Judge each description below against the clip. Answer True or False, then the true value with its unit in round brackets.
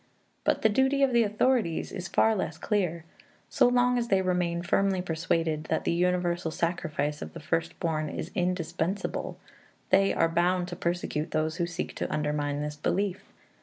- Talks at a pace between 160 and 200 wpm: True (170 wpm)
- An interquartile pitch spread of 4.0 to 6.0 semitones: False (3.4 semitones)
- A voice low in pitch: False (175 Hz)